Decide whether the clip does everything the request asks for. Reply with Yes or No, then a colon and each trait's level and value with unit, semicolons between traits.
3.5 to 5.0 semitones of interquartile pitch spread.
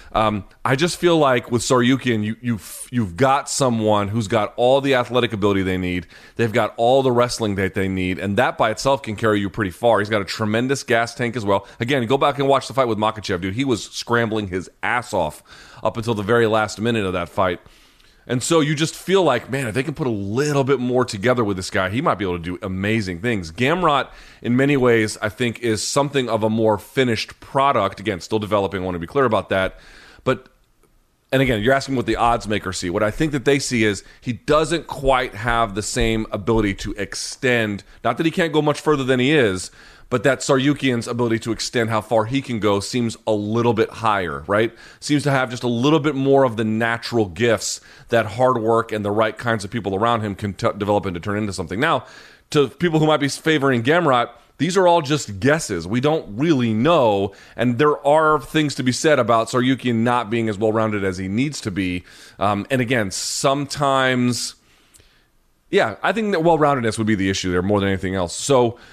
Yes: average, 4.1 semitones